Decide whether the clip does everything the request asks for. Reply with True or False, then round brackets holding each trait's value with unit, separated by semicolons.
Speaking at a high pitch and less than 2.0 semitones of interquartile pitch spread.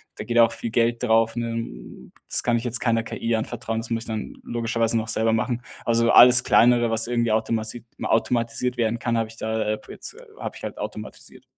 False (115 Hz; 0.9 semitones)